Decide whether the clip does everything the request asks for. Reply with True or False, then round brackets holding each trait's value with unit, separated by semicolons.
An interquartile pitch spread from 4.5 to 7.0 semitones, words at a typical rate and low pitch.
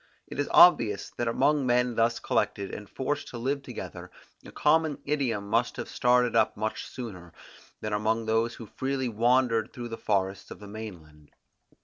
False (3.4 semitones; 175 wpm; 115 Hz)